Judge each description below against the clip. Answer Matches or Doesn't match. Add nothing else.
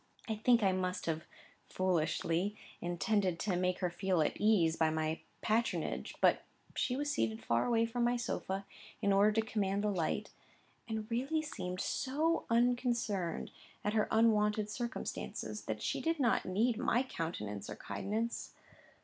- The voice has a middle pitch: Doesn't match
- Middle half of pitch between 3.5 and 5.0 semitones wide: Matches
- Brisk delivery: Doesn't match